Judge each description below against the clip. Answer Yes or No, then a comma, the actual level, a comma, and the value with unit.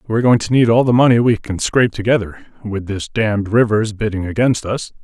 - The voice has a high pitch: No, low, 110 Hz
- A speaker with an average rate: No, fast, 215 wpm